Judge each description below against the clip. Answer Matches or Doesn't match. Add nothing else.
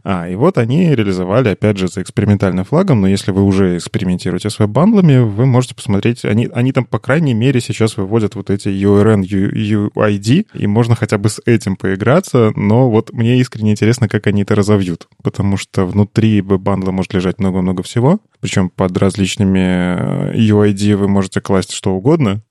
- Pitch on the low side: Matches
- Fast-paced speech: Matches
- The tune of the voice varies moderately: Matches